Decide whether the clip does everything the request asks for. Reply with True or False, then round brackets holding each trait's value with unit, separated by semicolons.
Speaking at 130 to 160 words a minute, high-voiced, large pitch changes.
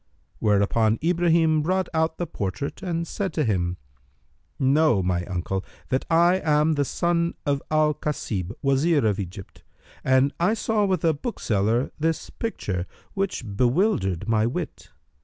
False (140 wpm; 145 Hz; 8.0 semitones)